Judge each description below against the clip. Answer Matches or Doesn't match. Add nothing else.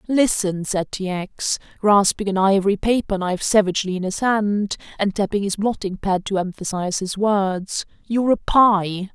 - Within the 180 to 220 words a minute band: Doesn't match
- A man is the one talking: Doesn't match